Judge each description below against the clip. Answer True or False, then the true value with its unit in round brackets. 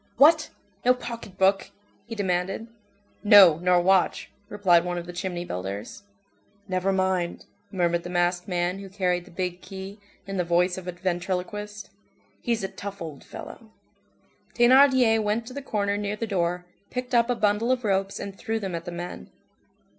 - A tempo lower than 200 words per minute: True (170 wpm)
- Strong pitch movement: False (3.1 semitones)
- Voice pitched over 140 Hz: True (190 Hz)